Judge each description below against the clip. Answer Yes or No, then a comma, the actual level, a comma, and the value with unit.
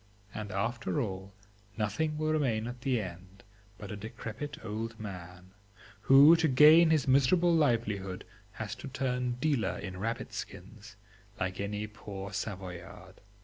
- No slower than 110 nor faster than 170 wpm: Yes, average, 140 wpm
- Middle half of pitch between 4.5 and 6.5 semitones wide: Yes, wide, 5.5 semitones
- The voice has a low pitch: Yes, low, 110 Hz